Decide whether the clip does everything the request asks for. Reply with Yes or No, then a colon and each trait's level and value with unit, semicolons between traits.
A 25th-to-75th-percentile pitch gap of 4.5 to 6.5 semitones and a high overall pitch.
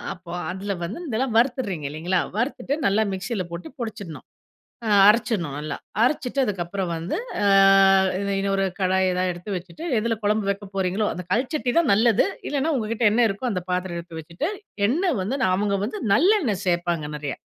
Yes: average, 4.8 semitones; high, 200 Hz